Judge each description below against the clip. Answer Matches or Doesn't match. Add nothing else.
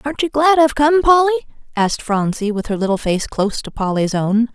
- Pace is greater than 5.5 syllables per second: Matches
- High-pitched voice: Matches